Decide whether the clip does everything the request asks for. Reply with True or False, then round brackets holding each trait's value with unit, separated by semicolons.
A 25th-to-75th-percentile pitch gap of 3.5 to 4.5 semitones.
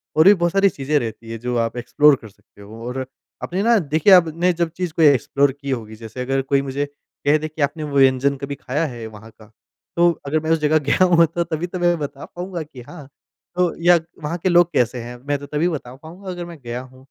False (5.2 semitones)